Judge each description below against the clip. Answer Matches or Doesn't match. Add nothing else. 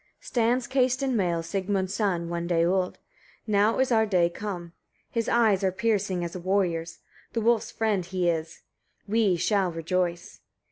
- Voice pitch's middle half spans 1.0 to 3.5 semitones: Doesn't match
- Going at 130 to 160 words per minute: Doesn't match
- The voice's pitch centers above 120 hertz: Matches